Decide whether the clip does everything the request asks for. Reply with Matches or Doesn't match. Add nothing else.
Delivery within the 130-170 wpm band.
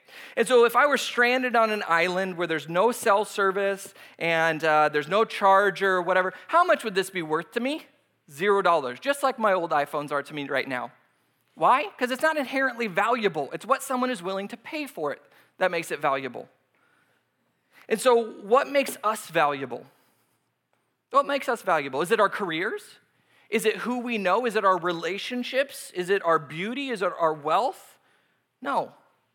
Doesn't match